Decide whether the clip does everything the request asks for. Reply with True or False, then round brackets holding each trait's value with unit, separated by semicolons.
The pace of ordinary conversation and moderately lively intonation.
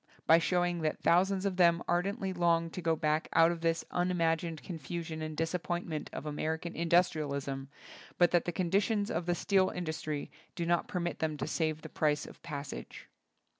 False (185 wpm; 2.0 semitones)